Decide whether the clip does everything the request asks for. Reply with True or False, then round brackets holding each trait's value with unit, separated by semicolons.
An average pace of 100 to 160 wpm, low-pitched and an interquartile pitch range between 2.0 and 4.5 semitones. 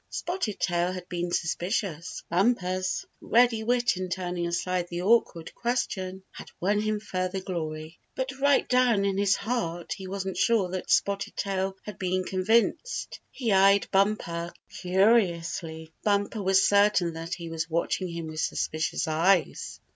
False (150 wpm; 190 Hz; 3.2 semitones)